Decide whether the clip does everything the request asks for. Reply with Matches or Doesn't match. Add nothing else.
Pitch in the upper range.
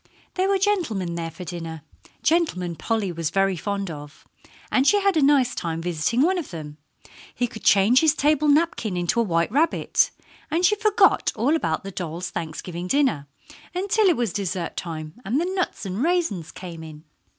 Matches